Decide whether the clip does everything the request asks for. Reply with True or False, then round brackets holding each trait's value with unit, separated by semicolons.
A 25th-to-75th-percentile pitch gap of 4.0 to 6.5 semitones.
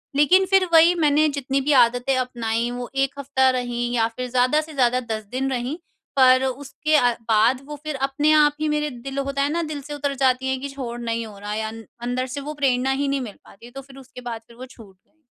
False (2.8 semitones)